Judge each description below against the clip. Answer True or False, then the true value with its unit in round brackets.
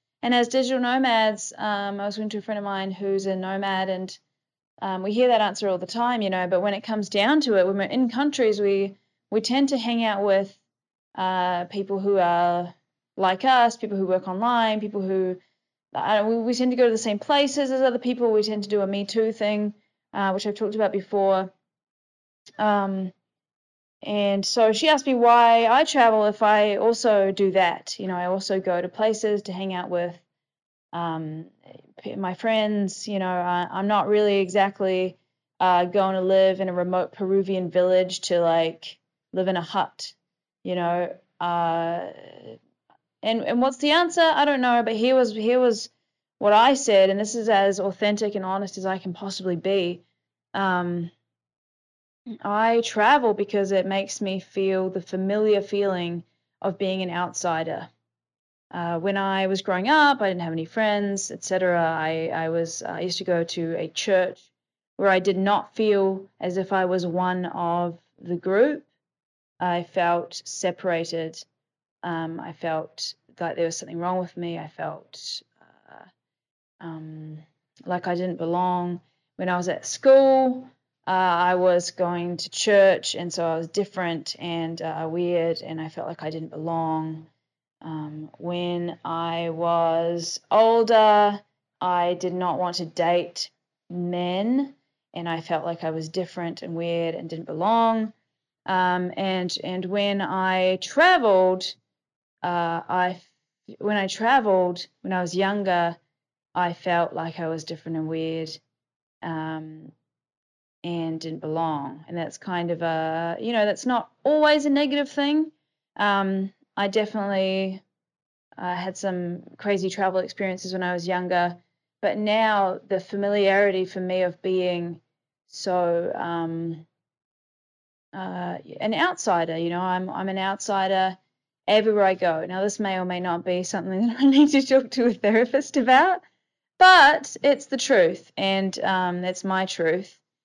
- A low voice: False (190 Hz)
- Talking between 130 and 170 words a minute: True (165 wpm)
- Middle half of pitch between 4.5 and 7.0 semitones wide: False (3.3 semitones)